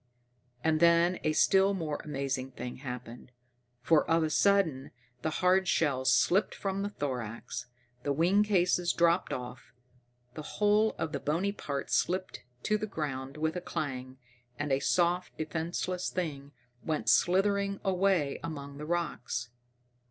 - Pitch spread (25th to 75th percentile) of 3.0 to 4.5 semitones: No, average, 4.9 semitones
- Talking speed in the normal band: Yes, average, 145 wpm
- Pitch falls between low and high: Yes, medium, 160 Hz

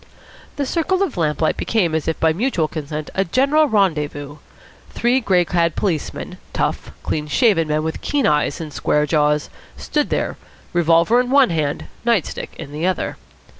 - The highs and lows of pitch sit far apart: Yes, wide, 7.5 semitones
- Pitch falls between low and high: Yes, medium, 170 Hz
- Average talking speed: Yes, average, 170 wpm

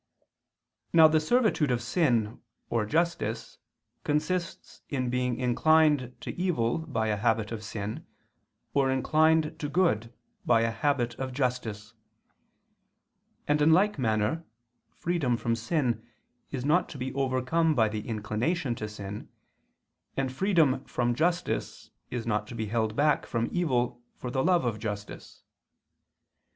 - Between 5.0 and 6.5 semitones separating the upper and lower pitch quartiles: Yes, wide, 5.6 semitones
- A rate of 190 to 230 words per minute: No, average, 140 wpm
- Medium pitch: No, low, 125 Hz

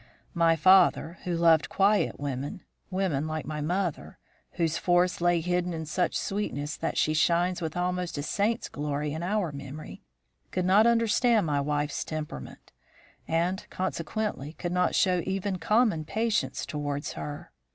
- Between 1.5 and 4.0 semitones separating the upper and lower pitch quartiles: Yes, average, 3.6 semitones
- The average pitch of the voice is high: No, medium, 170 Hz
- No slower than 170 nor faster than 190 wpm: No, average, 150 wpm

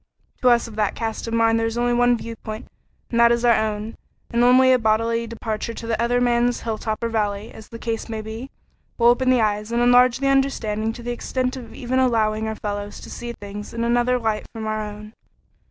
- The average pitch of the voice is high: Yes, high, 230 Hz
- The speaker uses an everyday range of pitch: No, narrow, 1.8 semitones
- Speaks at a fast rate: Yes, fast, 225 wpm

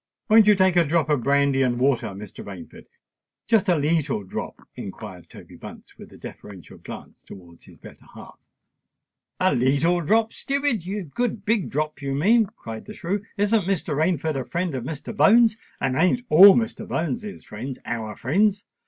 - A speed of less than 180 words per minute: Yes, average, 165 wpm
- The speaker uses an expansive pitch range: Yes, wide, 7.8 semitones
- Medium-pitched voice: Yes, medium, 160 Hz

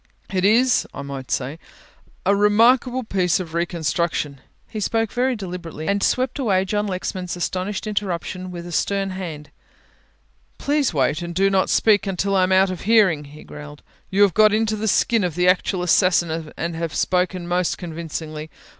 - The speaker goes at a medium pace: Yes, average, 170 wpm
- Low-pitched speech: No, medium, 185 Hz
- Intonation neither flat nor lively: Yes, average, 3.5 semitones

